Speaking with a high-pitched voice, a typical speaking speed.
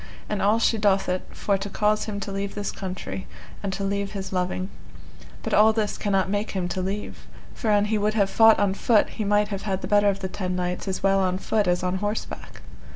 No: high, 200 Hz; fast, 235 wpm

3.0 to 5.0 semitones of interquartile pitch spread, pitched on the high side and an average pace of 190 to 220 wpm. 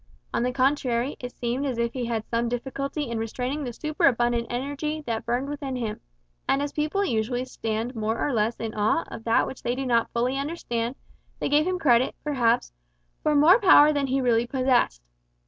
Yes: average, 3.4 semitones; very high, 250 Hz; average, 195 wpm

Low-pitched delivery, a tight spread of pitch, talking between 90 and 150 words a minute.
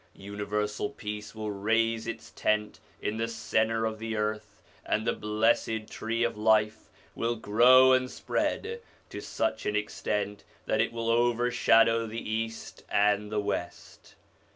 Yes: low, 110 Hz; narrow, 1.5 semitones; average, 145 wpm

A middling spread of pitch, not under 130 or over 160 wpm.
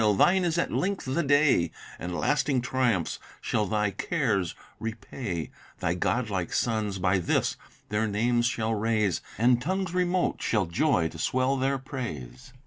No: wide, 5.7 semitones; average, 145 wpm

